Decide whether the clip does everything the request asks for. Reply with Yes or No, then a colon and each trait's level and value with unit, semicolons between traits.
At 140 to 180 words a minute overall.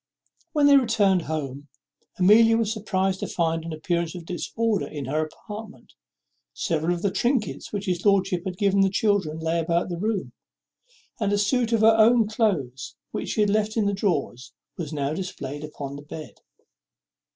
Yes: average, 175 wpm